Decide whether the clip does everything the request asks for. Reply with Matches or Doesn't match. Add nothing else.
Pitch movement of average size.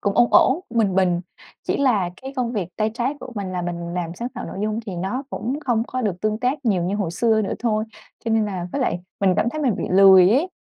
Matches